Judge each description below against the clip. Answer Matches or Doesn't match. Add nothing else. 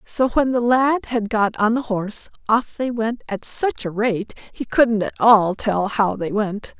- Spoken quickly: Matches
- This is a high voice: Matches